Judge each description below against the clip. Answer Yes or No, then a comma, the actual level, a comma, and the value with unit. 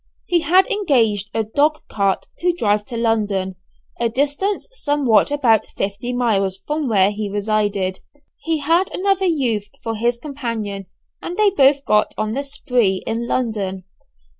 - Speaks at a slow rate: No, average, 150 wpm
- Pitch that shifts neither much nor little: No, wide, 5.9 semitones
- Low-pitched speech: No, high, 235 Hz